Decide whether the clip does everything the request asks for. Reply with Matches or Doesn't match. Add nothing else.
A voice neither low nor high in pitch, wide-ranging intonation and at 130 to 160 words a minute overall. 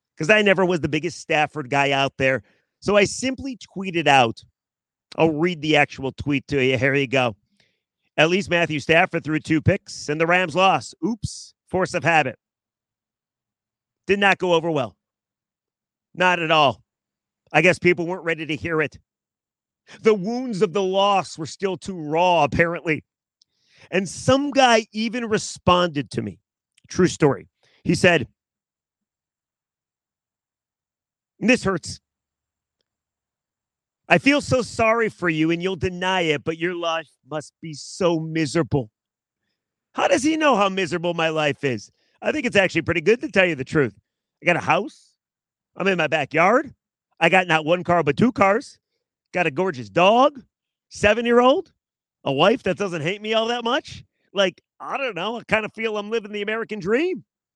Doesn't match